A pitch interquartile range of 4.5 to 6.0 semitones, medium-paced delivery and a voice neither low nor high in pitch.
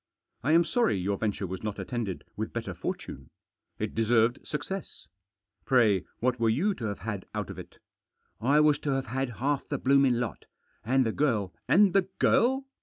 No: wide, 5.4 semitones; average, 195 wpm; low, 125 Hz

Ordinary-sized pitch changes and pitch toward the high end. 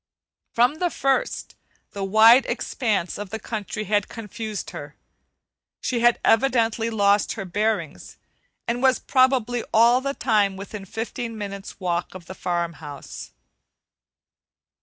Yes: average, 3.3 semitones; high, 220 Hz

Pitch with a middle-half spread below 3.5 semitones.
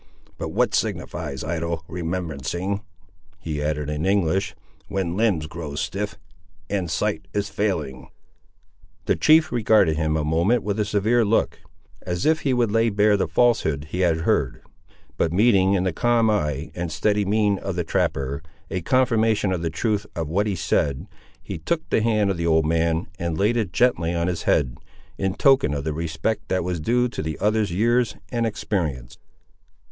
No: average, 5.1 semitones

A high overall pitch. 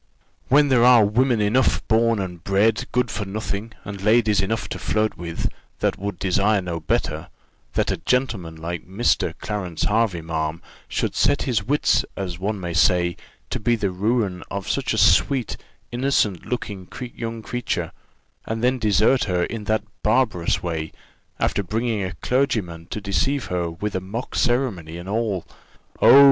No: low, 105 Hz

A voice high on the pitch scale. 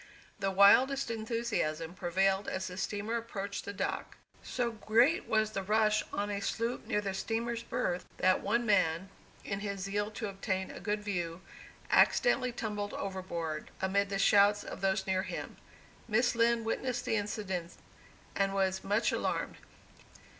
Yes: high, 205 Hz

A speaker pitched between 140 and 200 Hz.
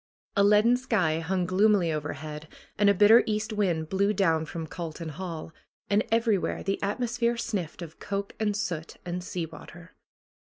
Yes: high, 190 Hz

